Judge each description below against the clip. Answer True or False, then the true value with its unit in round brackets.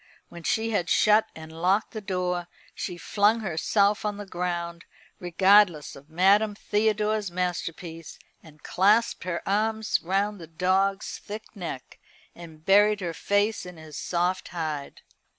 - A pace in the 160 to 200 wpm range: False (140 wpm)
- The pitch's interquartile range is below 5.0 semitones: True (3.4 semitones)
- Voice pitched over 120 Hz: True (185 Hz)